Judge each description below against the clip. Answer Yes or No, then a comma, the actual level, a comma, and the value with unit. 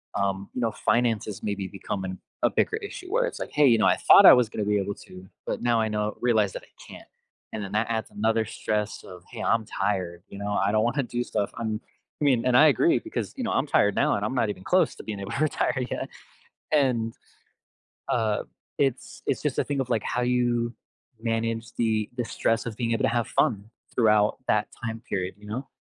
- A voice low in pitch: Yes, low, 115 Hz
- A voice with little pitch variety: No, average, 3.0 semitones